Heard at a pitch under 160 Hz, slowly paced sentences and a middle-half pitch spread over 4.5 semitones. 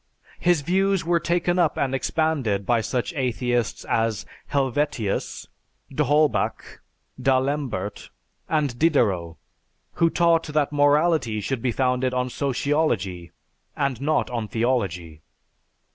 Yes: low, 135 Hz; slow, 110 wpm; average, 5.0 semitones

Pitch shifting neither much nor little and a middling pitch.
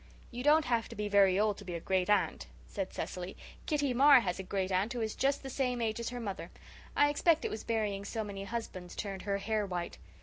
No: average, 4.3 semitones; high, 210 Hz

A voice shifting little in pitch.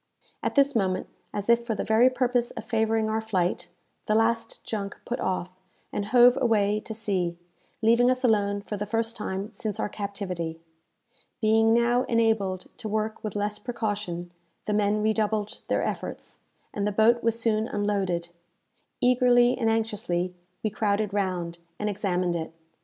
Yes: narrow, 2.3 semitones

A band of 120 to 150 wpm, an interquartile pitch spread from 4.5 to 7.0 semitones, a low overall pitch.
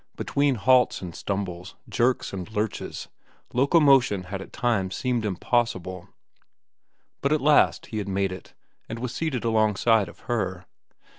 Yes: average, 140 wpm; average, 4.8 semitones; low, 110 Hz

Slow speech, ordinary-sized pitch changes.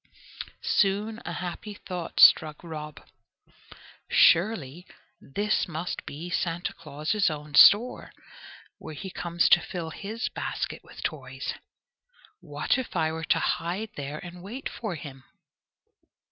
Yes: slow, 125 wpm; average, 4.6 semitones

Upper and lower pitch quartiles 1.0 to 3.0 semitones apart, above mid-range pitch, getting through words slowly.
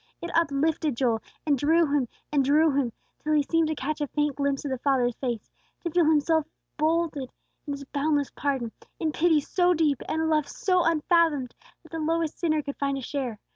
No: narrow, 2.6 semitones; very high, 295 Hz; average, 200 wpm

